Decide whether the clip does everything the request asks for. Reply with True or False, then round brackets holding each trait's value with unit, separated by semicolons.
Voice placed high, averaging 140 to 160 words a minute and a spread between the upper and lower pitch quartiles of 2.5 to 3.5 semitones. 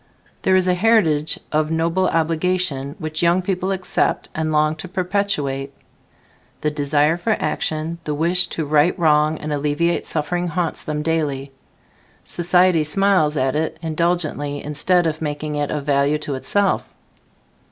False (155 Hz; 145 wpm; 3.0 semitones)